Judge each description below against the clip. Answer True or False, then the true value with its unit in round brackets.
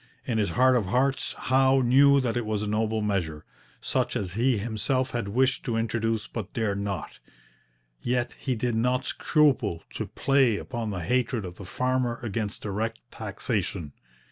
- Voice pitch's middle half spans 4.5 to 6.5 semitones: False (3.6 semitones)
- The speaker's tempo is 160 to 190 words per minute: True (170 wpm)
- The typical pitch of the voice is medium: False (115 Hz)